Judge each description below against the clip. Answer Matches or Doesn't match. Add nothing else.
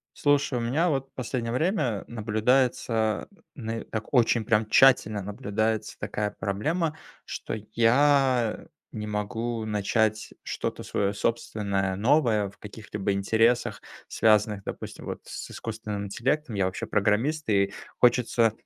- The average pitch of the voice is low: Matches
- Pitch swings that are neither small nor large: Matches